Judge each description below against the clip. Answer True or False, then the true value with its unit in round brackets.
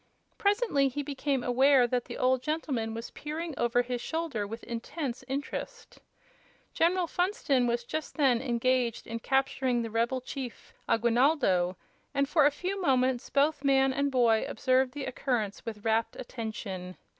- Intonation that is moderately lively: True (3.5 semitones)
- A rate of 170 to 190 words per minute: False (150 wpm)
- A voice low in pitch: False (255 Hz)